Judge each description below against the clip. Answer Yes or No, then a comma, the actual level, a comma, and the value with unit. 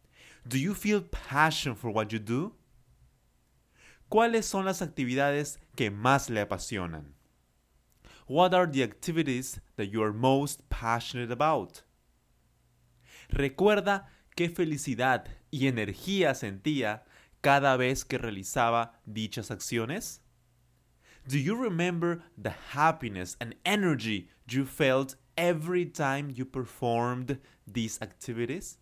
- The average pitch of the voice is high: No, low, 130 Hz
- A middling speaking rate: No, slow, 110 wpm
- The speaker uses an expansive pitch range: Yes, wide, 5.8 semitones